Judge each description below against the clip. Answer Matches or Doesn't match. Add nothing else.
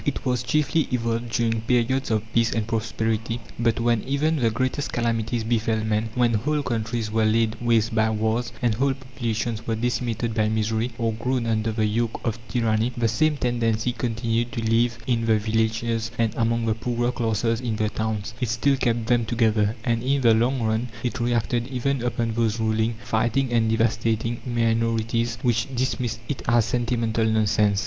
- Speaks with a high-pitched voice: Doesn't match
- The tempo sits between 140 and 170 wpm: Doesn't match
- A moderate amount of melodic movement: Doesn't match